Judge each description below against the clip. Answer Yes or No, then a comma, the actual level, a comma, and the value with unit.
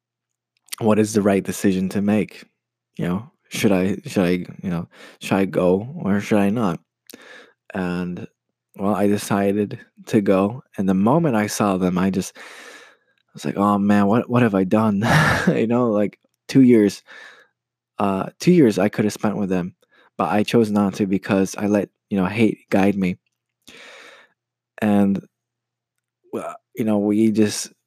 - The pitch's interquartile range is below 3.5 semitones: Yes, average, 2.9 semitones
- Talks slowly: No, average, 170 wpm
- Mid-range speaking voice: No, low, 105 Hz